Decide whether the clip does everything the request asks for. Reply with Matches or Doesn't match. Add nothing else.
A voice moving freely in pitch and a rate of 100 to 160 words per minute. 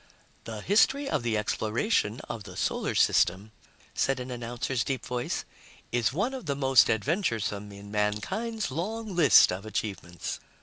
Matches